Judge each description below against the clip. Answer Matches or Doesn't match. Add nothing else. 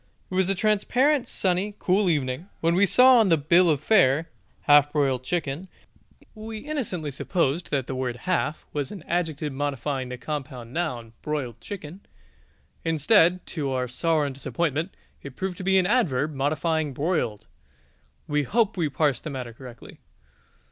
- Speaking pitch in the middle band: Matches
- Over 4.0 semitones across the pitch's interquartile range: Matches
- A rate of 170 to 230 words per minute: Doesn't match